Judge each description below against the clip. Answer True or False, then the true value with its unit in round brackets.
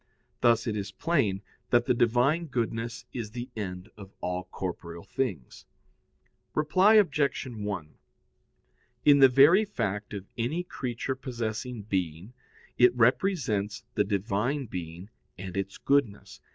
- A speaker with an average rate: False (125 wpm)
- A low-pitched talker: True (115 Hz)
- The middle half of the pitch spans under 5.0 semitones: False (5.3 semitones)